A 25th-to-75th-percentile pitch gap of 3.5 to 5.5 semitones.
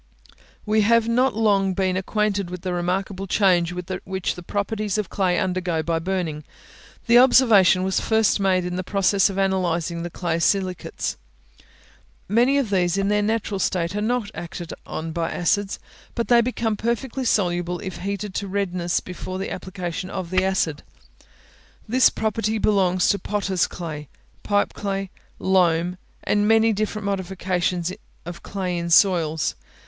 No: average, 2.8 semitones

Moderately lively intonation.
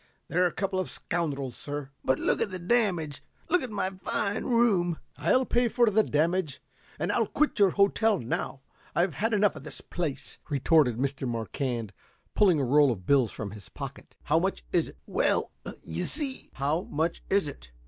No: wide, 6.8 semitones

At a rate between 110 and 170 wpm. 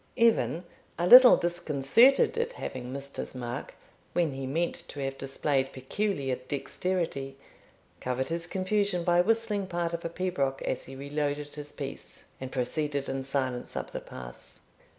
Yes: average, 150 wpm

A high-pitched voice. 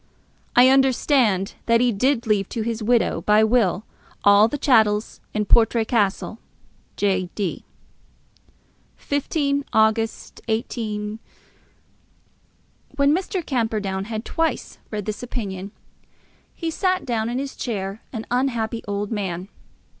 Yes: high, 225 Hz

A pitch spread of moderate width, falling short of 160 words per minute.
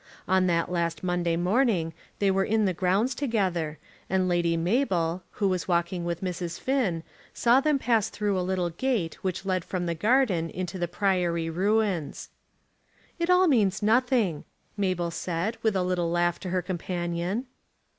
No: average, 3.6 semitones; average, 165 wpm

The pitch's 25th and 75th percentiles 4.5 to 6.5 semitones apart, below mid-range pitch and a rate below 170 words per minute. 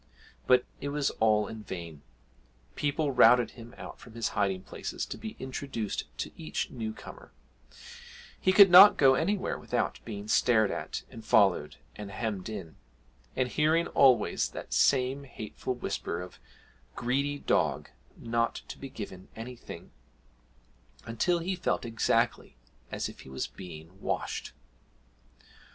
Yes: average, 5.0 semitones; low, 115 Hz; average, 140 wpm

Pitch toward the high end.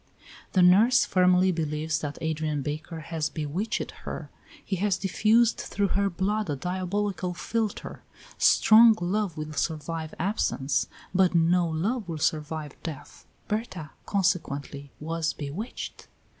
No: medium, 175 Hz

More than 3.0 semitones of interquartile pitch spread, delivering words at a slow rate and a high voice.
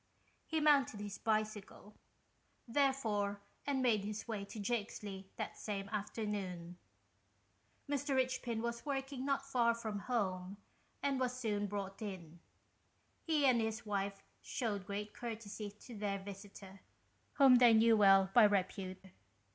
Yes: average, 3.6 semitones; slow, 130 wpm; high, 215 Hz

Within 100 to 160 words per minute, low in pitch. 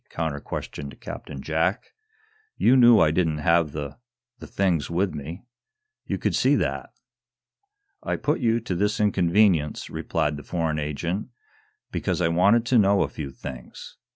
Yes: average, 155 wpm; very low, 85 Hz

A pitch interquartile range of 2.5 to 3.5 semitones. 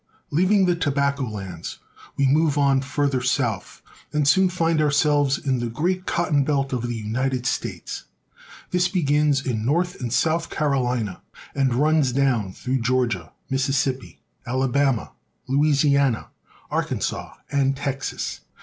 Yes: average, 2.9 semitones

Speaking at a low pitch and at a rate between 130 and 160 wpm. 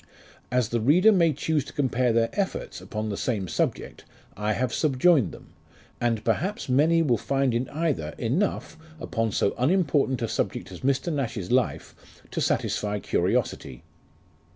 Yes: low, 130 Hz; average, 150 wpm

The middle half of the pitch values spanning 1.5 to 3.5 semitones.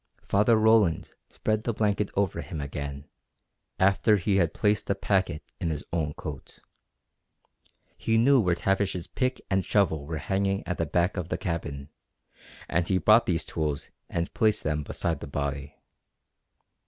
No: average, 4.8 semitones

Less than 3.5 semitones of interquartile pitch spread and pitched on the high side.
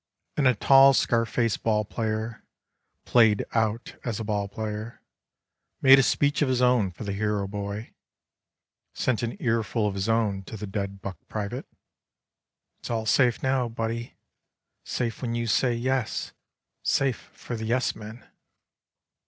No: average, 2.7 semitones; low, 115 Hz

